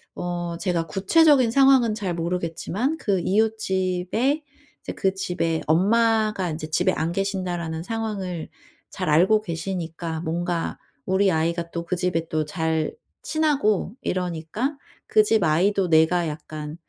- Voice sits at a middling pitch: Yes, medium, 180 Hz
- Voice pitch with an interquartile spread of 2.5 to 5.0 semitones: Yes, average, 4.3 semitones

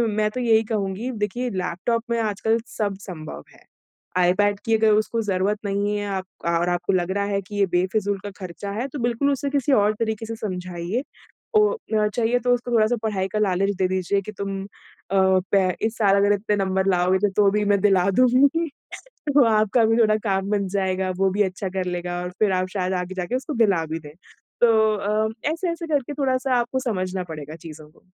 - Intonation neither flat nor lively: Yes, average, 3.2 semitones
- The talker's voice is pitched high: Yes, high, 200 Hz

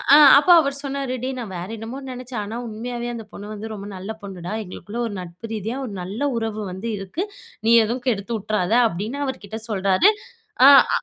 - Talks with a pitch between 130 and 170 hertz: No, high, 220 Hz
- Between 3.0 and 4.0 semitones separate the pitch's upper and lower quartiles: Yes, average, 3.7 semitones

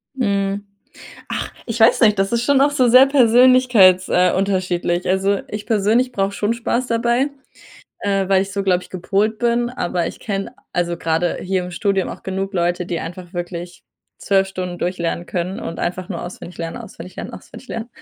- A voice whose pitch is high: Yes, high, 195 Hz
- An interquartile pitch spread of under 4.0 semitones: No, average, 4.3 semitones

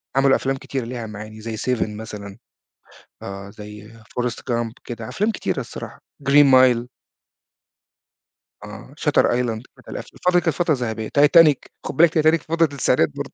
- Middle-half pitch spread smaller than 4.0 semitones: No, average, 4.7 semitones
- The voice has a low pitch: Yes, low, 120 Hz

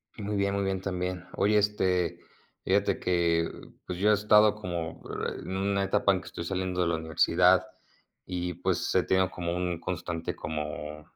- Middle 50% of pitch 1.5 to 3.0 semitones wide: Yes, narrow, 2.6 semitones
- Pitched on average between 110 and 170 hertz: No, very low, 90 Hz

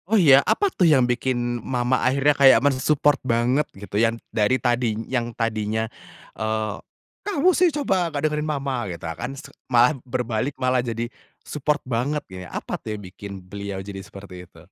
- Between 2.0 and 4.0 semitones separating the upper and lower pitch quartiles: No, average, 4.5 semitones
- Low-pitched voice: Yes, low, 125 Hz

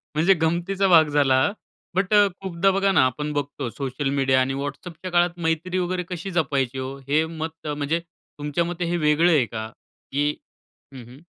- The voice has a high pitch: No, medium, 160 Hz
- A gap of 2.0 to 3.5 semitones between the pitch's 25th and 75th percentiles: No, average, 3.9 semitones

